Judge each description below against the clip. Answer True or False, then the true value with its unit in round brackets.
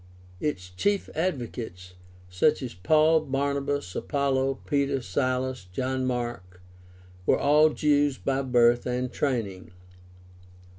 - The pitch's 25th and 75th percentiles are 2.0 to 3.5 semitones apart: True (3.1 semitones)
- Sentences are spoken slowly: True (105 wpm)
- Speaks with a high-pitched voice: False (130 Hz)